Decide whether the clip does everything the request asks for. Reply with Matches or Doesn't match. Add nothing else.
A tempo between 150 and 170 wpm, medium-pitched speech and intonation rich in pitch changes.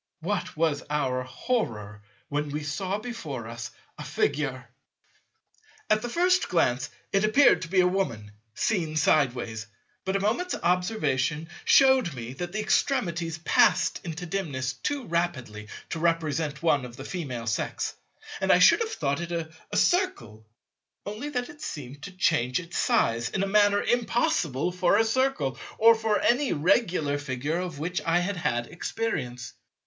Matches